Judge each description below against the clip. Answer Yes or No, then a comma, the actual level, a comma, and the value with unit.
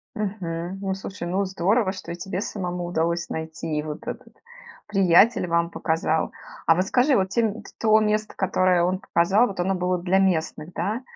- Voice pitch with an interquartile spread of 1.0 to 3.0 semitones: Yes, average, 2.7 semitones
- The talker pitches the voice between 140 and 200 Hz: Yes, medium, 185 Hz